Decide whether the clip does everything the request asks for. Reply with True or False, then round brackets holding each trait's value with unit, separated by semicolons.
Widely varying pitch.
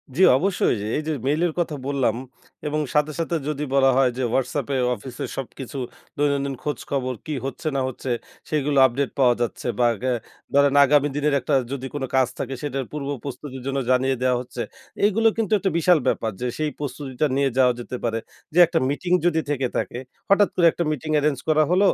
False (2.7 semitones)